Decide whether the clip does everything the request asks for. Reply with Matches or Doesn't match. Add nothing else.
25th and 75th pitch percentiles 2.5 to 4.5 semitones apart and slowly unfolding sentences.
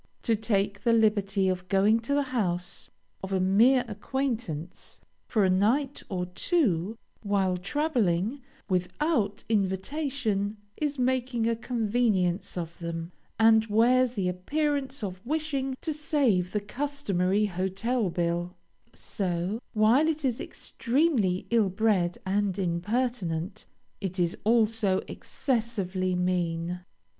Doesn't match